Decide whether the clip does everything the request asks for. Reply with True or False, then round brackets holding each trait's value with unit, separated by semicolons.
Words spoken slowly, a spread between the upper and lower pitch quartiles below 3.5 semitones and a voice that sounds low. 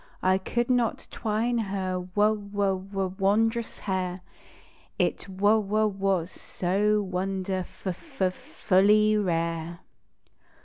False (115 wpm; 2.4 semitones; 195 Hz)